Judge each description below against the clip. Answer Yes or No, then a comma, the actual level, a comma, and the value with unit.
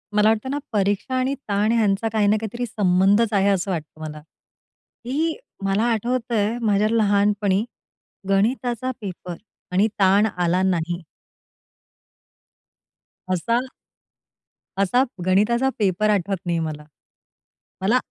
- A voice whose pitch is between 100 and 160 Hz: No, high, 205 Hz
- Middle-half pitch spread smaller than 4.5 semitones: Yes, average, 3.3 semitones